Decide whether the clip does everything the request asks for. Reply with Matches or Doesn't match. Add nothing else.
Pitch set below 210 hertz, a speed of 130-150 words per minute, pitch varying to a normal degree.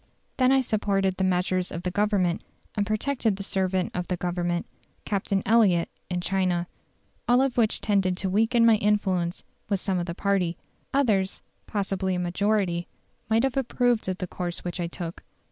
Doesn't match